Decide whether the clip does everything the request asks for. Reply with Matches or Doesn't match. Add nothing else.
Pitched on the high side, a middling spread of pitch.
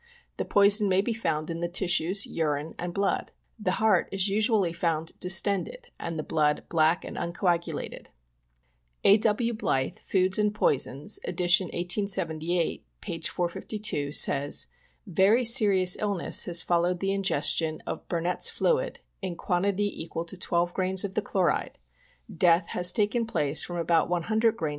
Doesn't match